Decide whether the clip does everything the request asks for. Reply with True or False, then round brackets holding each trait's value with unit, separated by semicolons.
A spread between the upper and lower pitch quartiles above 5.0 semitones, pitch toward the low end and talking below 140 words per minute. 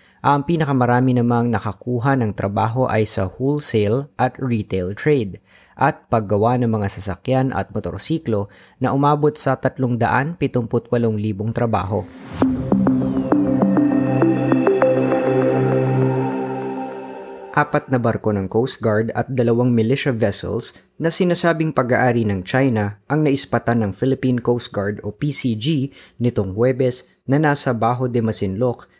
False (4.7 semitones; 120 Hz; 110 wpm)